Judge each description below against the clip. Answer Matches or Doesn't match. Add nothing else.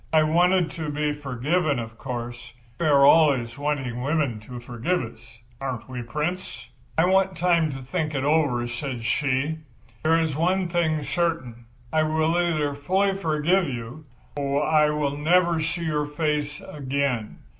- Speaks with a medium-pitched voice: Matches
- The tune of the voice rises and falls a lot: Doesn't match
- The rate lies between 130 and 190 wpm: Matches